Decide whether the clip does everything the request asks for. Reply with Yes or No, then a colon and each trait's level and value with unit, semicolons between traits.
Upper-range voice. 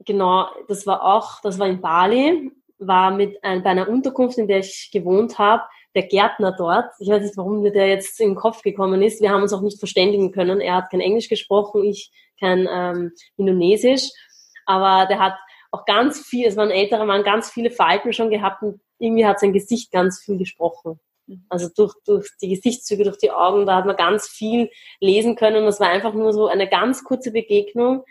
Yes: high, 205 Hz